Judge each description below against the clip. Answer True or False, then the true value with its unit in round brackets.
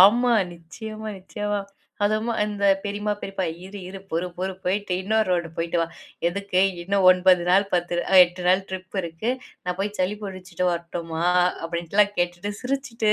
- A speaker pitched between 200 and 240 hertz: False (190 Hz)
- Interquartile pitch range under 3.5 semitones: True (2.9 semitones)